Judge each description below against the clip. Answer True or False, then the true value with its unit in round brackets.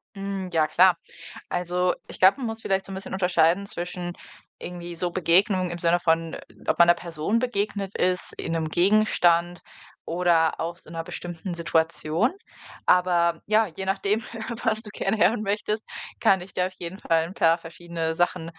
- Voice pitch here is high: False (175 Hz)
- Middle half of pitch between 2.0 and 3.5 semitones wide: True (2.6 semitones)